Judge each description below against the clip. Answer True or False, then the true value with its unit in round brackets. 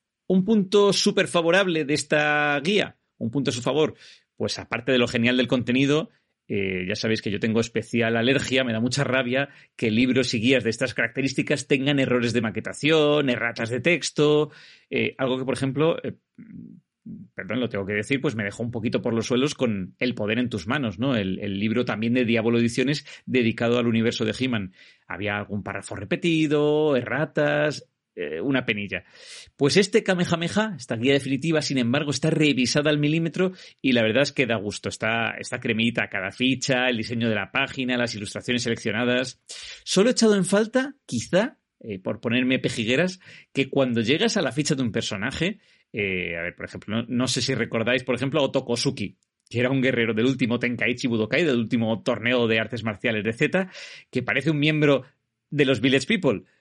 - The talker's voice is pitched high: False (125 Hz)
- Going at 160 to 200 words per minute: True (190 wpm)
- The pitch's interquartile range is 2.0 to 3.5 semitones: False (4.3 semitones)